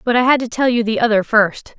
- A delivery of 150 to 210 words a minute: No, fast, 305 wpm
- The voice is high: Yes, high, 230 Hz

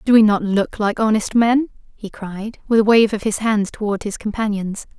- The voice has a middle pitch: No, high, 215 Hz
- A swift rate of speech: Yes, fast, 215 wpm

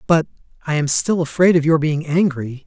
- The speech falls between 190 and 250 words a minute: Yes, average, 200 wpm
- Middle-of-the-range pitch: Yes, medium, 155 Hz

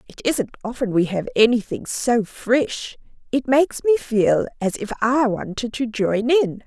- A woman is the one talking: Yes, female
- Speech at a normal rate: Yes, average, 170 wpm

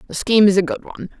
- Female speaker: Yes, female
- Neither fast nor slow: No, fast, 300 wpm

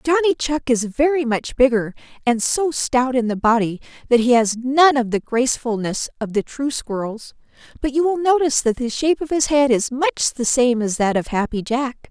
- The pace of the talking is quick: Yes, fast, 210 wpm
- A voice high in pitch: Yes, very high, 255 Hz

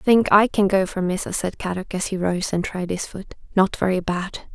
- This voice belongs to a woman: Yes, female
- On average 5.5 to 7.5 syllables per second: No, 4.9 syllables/s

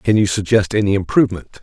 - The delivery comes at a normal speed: Yes, average, 185 wpm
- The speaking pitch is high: No, low, 100 Hz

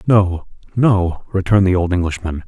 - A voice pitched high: No, very low, 95 Hz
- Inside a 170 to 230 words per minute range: No, slow, 120 wpm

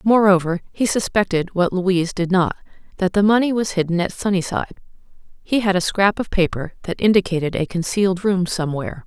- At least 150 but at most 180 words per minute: Yes, average, 170 wpm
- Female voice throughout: Yes, female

